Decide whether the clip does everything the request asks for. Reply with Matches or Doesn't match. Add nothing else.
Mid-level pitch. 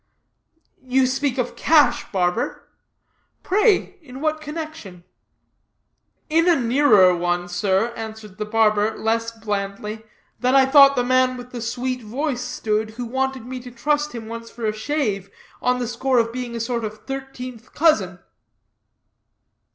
Doesn't match